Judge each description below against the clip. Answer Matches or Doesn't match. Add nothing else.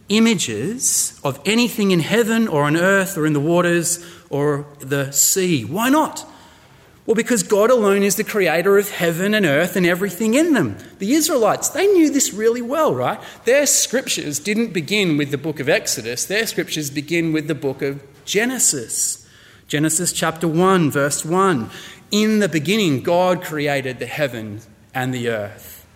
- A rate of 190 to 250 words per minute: Doesn't match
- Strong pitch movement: Matches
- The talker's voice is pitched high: Doesn't match